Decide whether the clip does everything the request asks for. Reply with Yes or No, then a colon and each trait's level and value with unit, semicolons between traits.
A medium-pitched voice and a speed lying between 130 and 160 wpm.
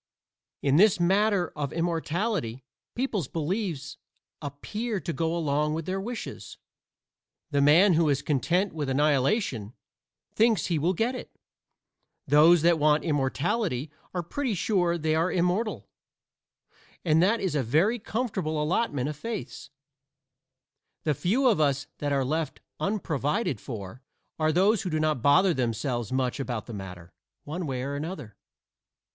Yes: medium, 160 Hz; average, 140 wpm